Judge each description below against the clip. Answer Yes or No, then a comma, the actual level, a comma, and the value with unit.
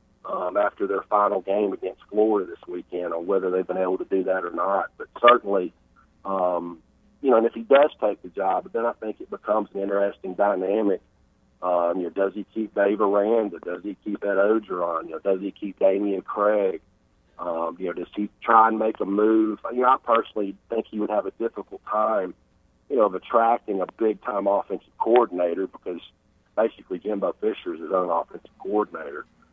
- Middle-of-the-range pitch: No, low, 100 Hz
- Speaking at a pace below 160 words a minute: No, fast, 205 wpm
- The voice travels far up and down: No, average, 2.8 semitones